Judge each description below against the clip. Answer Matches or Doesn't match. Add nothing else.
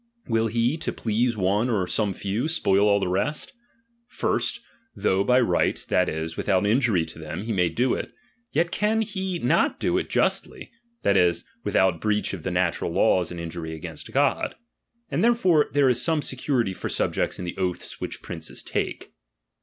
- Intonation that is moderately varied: Doesn't match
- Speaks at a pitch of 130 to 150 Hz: Doesn't match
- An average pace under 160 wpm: Doesn't match